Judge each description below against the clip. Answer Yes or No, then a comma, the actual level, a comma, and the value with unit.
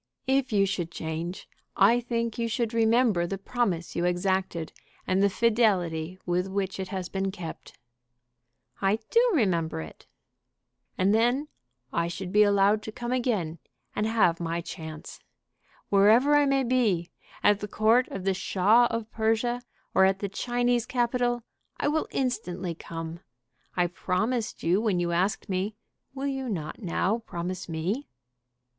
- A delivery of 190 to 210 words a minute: No, average, 150 wpm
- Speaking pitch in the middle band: No, high, 200 Hz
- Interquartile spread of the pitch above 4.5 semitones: Yes, average, 5.0 semitones